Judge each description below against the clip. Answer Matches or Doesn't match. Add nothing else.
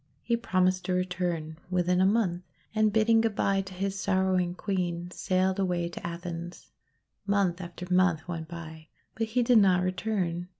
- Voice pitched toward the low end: Doesn't match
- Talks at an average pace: Matches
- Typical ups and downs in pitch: Doesn't match